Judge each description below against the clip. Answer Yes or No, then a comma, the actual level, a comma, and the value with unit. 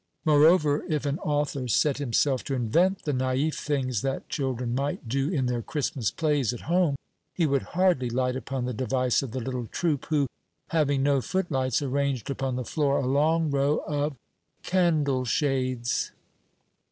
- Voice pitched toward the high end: No, medium, 140 Hz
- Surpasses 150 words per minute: Yes, average, 165 wpm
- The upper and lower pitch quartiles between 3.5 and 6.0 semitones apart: No, average, 2.8 semitones